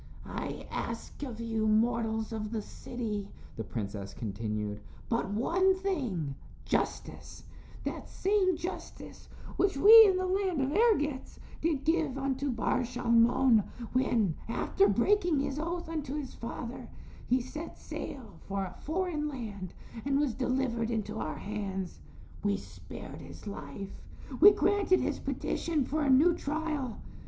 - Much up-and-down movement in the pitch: Yes, wide, 6.6 semitones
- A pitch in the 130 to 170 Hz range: No, very high, 255 Hz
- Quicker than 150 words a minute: No, average, 140 wpm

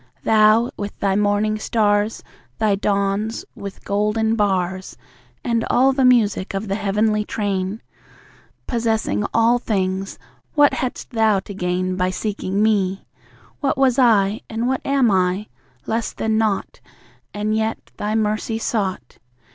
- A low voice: No, high, 210 Hz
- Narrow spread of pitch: Yes, narrow, 2.2 semitones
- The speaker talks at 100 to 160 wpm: Yes, slow, 135 wpm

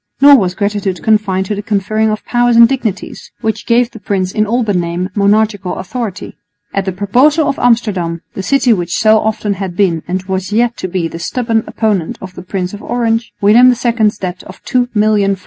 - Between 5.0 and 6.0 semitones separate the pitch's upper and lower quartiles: No, average, 3.5 semitones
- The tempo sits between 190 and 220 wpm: Yes, average, 200 wpm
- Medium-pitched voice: No, high, 210 Hz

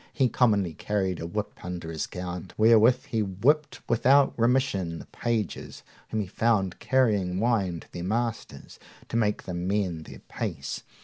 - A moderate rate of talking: Yes, average, 160 wpm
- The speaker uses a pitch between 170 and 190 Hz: No, low, 105 Hz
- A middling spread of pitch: Yes, average, 4.5 semitones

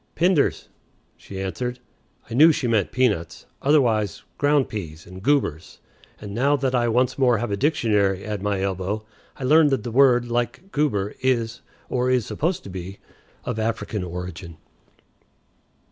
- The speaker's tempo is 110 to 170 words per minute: Yes, average, 155 wpm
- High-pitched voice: No, low, 115 Hz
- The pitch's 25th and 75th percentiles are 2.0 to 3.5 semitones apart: No, average, 5.0 semitones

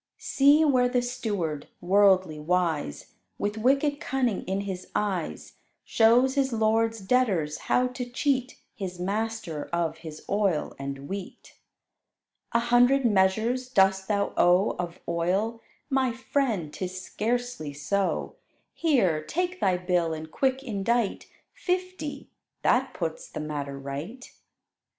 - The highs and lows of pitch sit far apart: Yes, wide, 6.0 semitones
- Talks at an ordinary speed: No, slow, 125 wpm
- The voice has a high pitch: Yes, high, 205 Hz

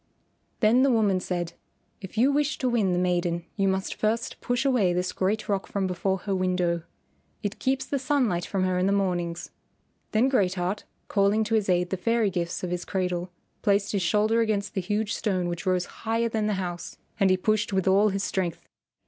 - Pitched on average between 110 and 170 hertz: No, high, 195 Hz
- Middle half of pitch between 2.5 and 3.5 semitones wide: Yes, average, 3.2 semitones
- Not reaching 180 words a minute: No, fast, 205 wpm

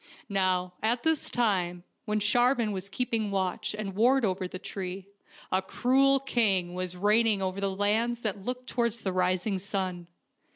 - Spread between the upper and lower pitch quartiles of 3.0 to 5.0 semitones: Yes, average, 4.0 semitones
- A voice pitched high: Yes, high, 200 Hz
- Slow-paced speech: No, average, 160 wpm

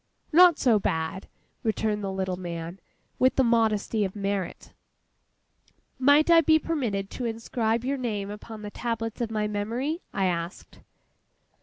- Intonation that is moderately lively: Yes, average, 4.1 semitones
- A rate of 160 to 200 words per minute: No, average, 145 wpm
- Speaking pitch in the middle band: No, high, 220 Hz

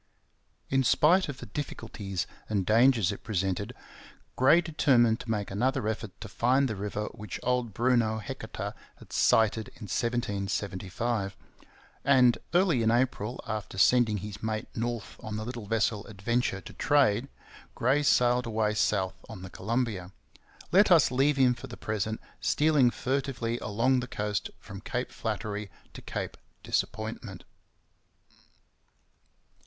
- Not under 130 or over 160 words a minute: Yes, average, 140 wpm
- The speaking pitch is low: Yes, low, 115 Hz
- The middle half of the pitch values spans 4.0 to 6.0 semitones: No, average, 3.4 semitones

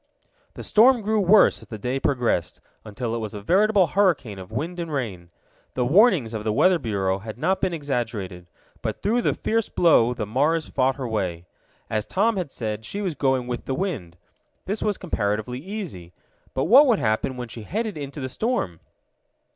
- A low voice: Yes, low, 130 Hz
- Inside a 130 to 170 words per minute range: No, average, 190 wpm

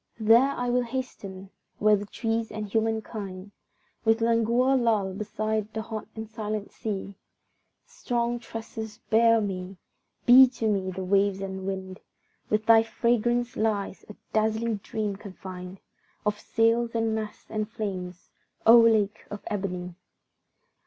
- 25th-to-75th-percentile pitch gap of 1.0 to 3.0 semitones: Yes, narrow, 2.5 semitones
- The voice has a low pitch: No, high, 215 Hz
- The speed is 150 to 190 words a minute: No, slow, 135 wpm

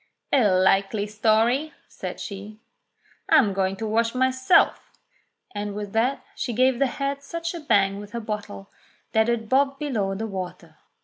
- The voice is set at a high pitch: Yes, high, 220 Hz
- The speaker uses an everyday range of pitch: Yes, average, 4.4 semitones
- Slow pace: No, average, 160 wpm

